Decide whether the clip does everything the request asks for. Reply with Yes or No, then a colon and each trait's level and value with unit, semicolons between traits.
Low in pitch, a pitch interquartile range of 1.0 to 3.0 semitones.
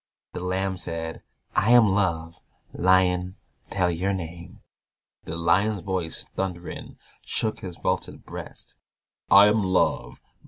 Yes: very low, 90 Hz; narrow, 2.5 semitones